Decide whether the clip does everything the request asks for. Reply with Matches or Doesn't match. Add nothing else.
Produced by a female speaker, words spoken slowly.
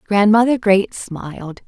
Matches